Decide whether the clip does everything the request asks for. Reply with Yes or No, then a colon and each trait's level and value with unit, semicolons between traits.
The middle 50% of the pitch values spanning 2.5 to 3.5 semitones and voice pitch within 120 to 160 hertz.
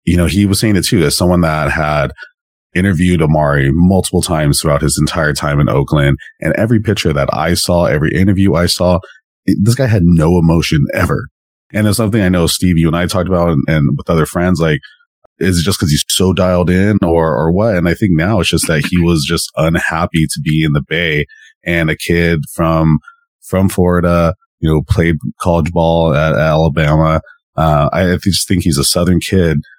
No: average, 2.9 semitones; very low, 85 Hz